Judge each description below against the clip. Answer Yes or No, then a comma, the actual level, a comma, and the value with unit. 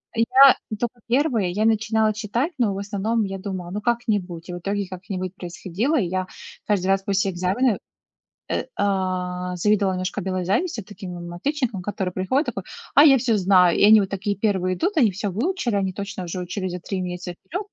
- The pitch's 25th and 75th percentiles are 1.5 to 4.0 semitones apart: Yes, average, 3.4 semitones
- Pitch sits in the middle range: No, high, 200 Hz